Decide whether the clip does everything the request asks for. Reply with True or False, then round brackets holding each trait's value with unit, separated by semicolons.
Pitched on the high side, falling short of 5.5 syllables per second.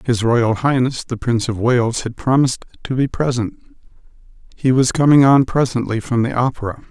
False (125 Hz; 5.2 syllables/s)